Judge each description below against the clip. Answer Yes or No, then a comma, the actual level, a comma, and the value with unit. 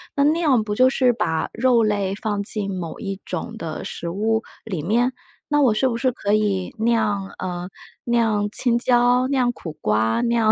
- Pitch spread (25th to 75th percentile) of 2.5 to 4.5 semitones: Yes, average, 3.7 semitones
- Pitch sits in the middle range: No, high, 220 Hz